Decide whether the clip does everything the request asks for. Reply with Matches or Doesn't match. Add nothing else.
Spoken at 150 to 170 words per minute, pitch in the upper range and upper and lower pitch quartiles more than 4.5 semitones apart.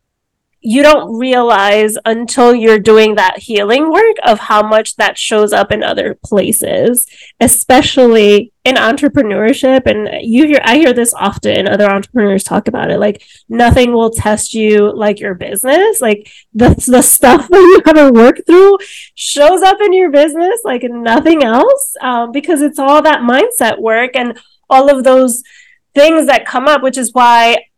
Matches